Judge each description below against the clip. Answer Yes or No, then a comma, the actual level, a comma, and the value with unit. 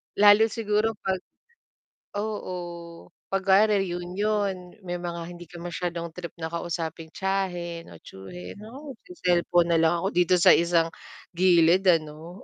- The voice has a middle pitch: Yes, medium, 175 Hz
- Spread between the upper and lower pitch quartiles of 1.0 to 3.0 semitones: Yes, narrow, 2.5 semitones